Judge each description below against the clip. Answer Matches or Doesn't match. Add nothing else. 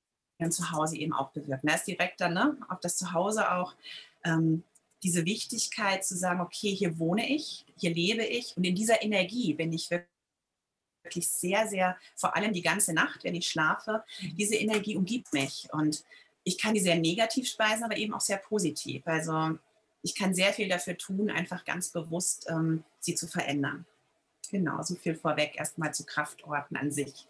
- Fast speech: Doesn't match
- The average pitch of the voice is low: Doesn't match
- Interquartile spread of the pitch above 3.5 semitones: Matches